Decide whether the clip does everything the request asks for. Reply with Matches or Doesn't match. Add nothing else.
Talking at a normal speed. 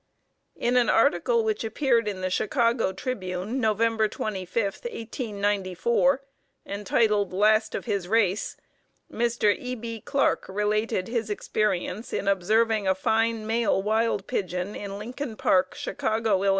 Doesn't match